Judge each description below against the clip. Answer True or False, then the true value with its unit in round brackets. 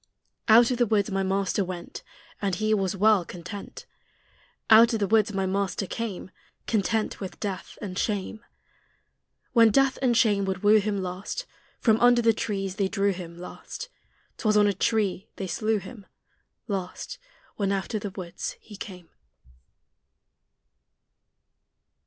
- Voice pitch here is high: True (205 Hz)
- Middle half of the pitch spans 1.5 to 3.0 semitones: True (2.5 semitones)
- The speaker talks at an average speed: True (150 wpm)